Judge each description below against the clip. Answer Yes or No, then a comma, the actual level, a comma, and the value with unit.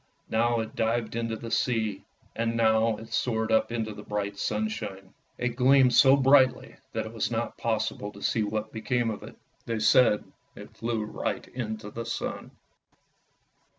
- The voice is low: Yes, low, 115 Hz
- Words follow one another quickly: No, average, 165 wpm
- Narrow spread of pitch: Yes, narrow, 1.6 semitones